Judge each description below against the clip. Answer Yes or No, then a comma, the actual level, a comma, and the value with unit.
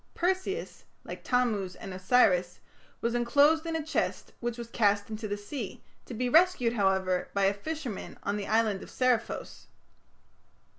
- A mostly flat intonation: No, average, 4.7 semitones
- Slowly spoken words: No, average, 155 wpm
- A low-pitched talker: No, high, 230 Hz